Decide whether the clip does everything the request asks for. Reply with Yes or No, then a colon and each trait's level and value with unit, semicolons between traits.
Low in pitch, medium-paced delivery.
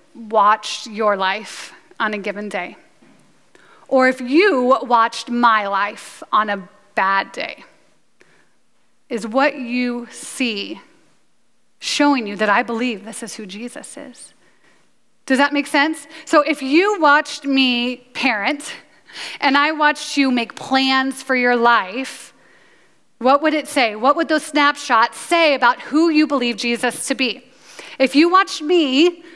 No: very high, 260 Hz; average, 145 wpm